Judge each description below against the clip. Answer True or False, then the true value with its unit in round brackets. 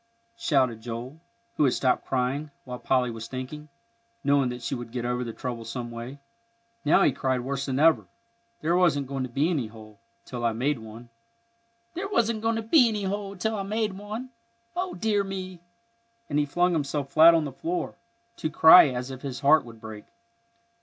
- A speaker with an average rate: True (160 wpm)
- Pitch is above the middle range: False (140 Hz)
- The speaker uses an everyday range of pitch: False (7.7 semitones)